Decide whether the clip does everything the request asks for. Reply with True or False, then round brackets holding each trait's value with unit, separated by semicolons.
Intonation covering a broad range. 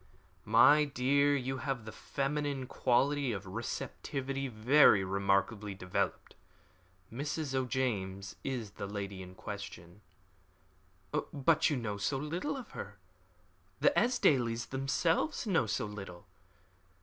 True (5.9 semitones)